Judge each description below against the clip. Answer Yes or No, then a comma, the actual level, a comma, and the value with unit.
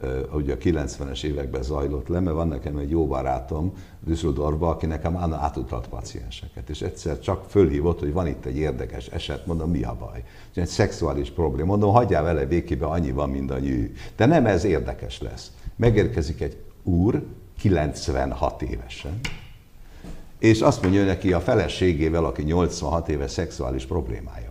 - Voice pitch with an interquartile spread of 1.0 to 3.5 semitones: No, average, 4.2 semitones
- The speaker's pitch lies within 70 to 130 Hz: Yes, very low, 85 Hz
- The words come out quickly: Yes, fast, 160 wpm